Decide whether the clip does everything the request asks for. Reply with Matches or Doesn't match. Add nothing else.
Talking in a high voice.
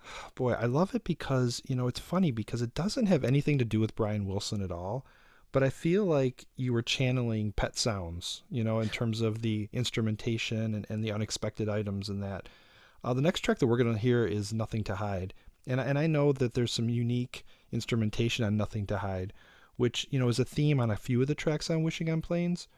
Doesn't match